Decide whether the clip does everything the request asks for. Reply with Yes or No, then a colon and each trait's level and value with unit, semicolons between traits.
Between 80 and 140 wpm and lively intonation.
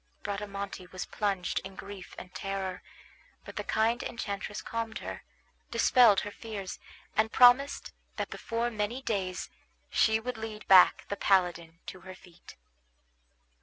No: slow, 135 wpm; average, 3.0 semitones